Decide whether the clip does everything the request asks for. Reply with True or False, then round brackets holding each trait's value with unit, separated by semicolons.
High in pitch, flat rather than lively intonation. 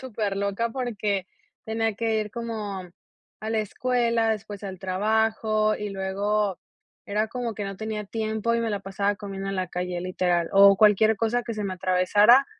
True (210 Hz; 2.2 semitones)